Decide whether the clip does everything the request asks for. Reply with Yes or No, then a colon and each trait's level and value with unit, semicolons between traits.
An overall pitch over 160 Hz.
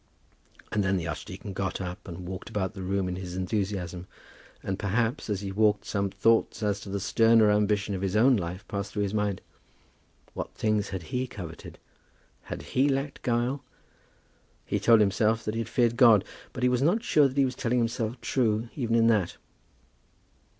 No: low, 105 Hz